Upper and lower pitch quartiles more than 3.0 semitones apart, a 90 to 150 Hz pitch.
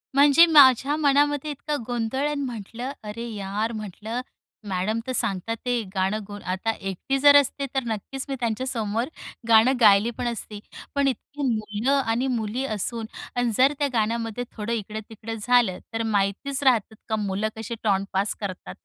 No: average, 4.0 semitones; high, 230 Hz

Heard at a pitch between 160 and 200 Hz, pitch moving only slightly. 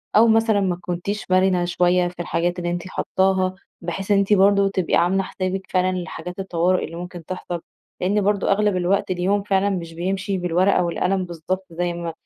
Yes: medium, 185 Hz; narrow, 1.8 semitones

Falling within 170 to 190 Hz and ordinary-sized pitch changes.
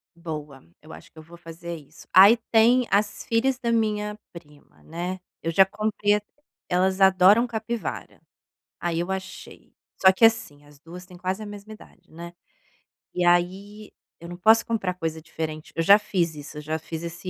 Yes: medium, 185 Hz; average, 4.1 semitones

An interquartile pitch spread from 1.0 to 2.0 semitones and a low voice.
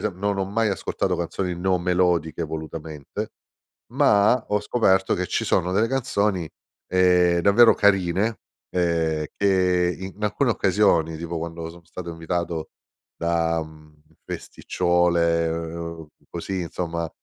No: narrow, 2.6 semitones; very low, 90 Hz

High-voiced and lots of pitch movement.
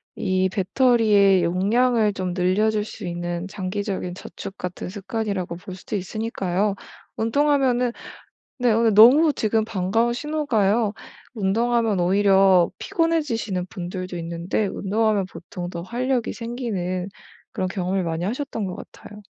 No: high, 205 Hz; average, 3.9 semitones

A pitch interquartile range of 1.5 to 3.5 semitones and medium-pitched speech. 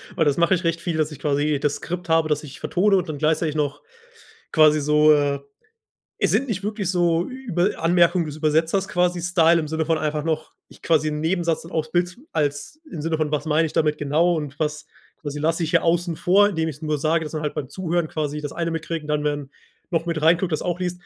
Yes: narrow, 2.5 semitones; medium, 160 Hz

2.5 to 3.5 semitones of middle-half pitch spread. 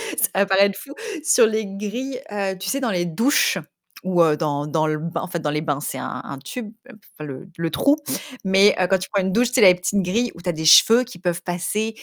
No: average, 4.5 semitones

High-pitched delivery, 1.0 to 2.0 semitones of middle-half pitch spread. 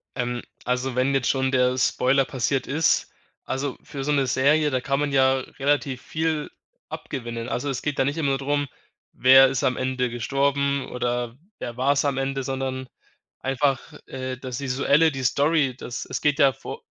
No: low, 135 Hz; narrow, 1.7 semitones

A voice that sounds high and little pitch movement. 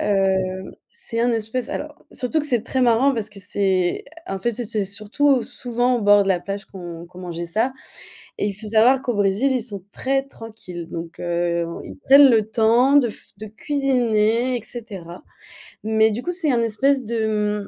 No: high, 220 Hz; average, 4.2 semitones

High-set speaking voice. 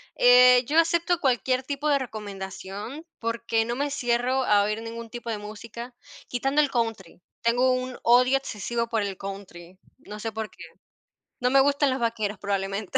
Yes: high, 235 Hz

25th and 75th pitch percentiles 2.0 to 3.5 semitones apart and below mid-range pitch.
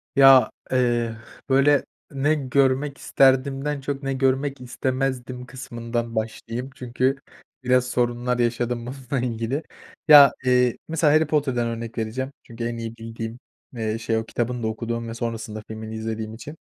Yes: narrow, 2.6 semitones; low, 125 Hz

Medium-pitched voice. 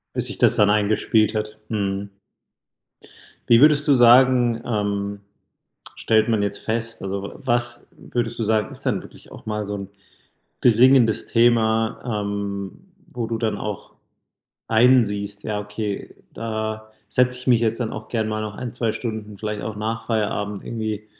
No: low, 110 Hz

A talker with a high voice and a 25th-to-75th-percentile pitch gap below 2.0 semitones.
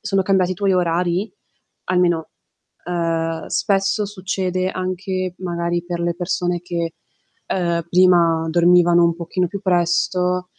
No: medium, 180 Hz; narrow, 1.4 semitones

